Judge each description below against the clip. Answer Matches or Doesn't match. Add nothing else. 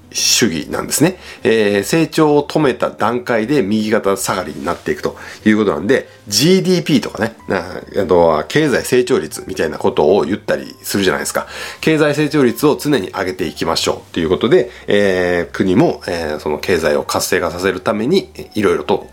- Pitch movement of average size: Doesn't match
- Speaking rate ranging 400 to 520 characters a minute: Doesn't match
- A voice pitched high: Doesn't match